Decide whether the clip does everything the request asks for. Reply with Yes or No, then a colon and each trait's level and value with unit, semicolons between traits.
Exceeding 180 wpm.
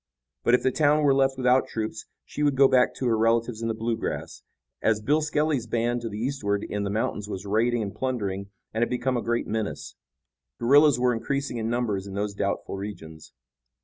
Yes: fast, 205 wpm